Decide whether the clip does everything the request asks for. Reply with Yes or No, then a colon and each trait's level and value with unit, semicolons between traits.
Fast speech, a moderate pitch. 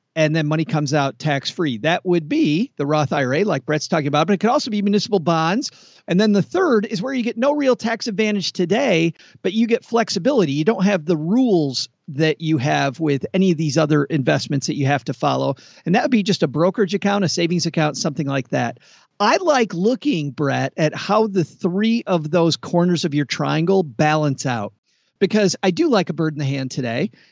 Yes: fast, 220 wpm; medium, 165 Hz